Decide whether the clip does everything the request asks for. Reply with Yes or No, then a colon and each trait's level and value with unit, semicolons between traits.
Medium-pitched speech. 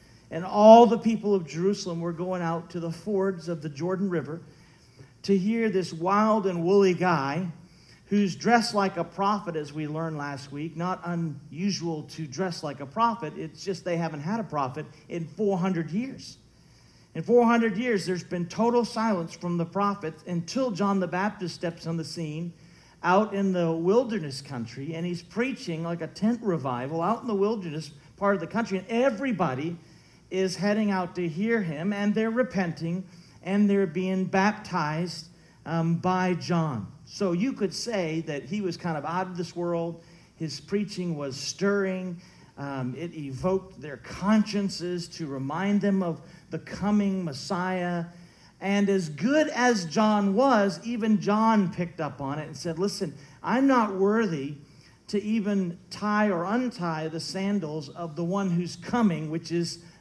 Yes: medium, 180 Hz